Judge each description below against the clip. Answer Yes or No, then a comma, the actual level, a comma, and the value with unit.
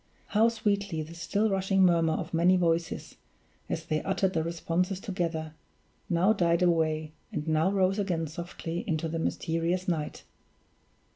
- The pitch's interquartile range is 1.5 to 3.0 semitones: Yes, average, 2.7 semitones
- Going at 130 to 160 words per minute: Yes, average, 145 wpm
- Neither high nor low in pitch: Yes, medium, 170 Hz